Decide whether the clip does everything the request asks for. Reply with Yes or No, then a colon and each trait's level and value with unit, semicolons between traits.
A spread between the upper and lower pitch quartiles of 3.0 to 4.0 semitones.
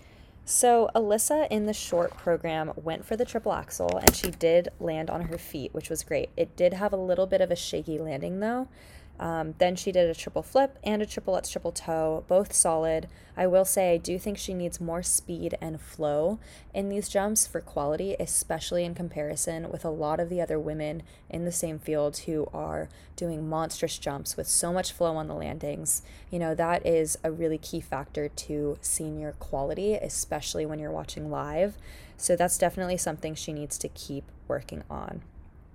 Yes: average, 3.3 semitones